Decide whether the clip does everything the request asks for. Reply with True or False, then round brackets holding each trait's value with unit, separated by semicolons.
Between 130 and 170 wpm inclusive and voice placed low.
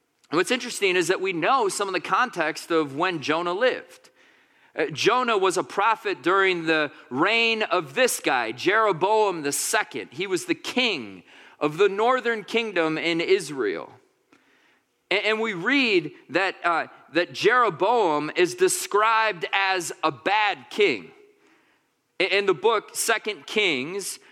False (135 wpm; 225 Hz)